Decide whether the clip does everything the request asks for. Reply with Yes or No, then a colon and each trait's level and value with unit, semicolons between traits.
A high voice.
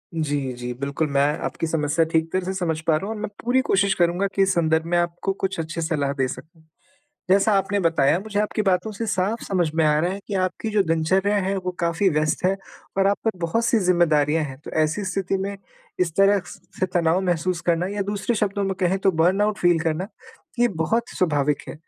No: medium, 180 Hz